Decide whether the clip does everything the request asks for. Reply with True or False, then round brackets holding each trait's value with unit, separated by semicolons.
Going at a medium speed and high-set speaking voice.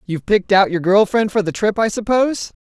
False (250 wpm; 205 Hz)